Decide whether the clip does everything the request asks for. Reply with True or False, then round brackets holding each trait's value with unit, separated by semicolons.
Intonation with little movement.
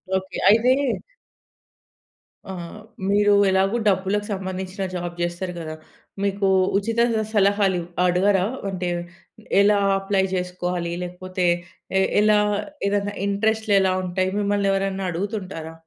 True (2.0 semitones)